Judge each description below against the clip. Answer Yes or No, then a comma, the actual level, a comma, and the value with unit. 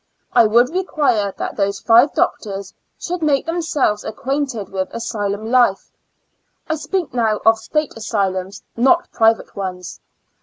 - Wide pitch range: Yes, wide, 6.0 semitones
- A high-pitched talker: Yes, high, 230 Hz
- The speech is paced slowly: Yes, slow, 130 wpm